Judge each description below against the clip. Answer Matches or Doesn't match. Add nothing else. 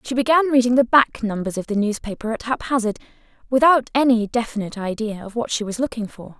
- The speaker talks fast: Doesn't match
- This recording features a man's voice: Doesn't match